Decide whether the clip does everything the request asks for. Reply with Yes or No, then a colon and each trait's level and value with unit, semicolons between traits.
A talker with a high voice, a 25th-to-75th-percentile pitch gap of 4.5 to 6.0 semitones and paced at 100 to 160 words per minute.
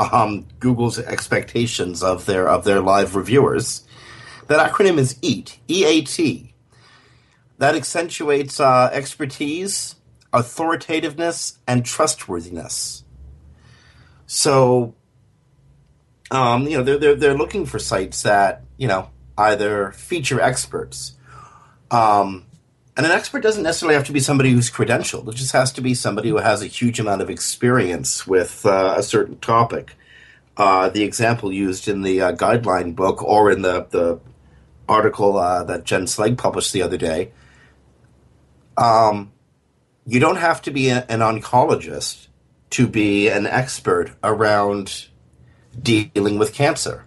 No: low, 120 Hz; wide, 5.4 semitones; slow, 135 wpm